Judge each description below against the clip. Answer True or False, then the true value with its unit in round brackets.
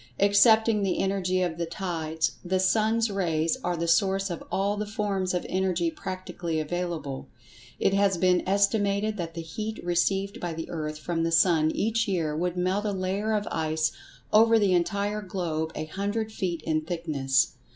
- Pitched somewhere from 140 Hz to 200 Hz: True (185 Hz)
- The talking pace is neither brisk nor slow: True (170 wpm)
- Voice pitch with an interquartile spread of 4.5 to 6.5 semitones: False (3.4 semitones)